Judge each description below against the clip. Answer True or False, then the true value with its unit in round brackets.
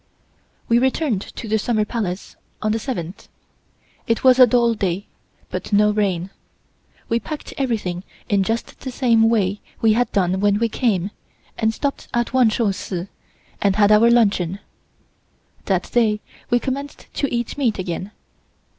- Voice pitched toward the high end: True (220 Hz)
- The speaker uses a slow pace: False (155 wpm)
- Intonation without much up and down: False (3.3 semitones)